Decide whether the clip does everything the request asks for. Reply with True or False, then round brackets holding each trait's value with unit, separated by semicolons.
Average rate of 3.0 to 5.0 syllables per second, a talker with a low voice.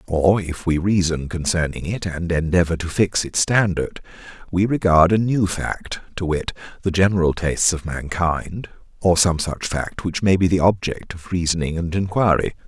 True (4.7 syllables/s; 85 Hz)